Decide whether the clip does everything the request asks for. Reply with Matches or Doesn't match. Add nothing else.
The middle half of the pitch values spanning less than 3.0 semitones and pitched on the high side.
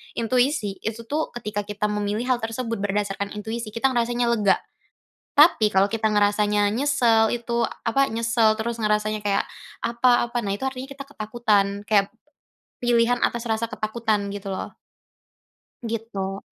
Matches